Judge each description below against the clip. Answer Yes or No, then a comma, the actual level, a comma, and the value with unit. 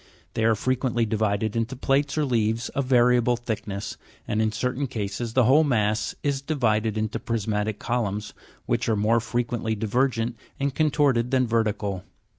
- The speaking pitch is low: Yes, low, 115 Hz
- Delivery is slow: No, average, 155 wpm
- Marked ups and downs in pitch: No, average, 2.9 semitones